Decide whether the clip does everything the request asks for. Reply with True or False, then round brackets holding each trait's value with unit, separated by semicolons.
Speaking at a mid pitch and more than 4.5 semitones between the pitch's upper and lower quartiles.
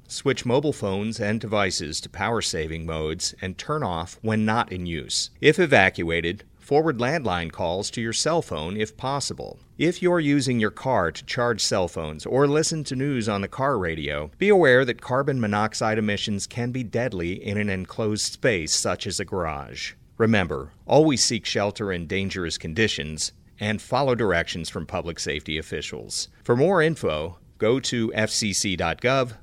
False (105 Hz; 5.2 semitones)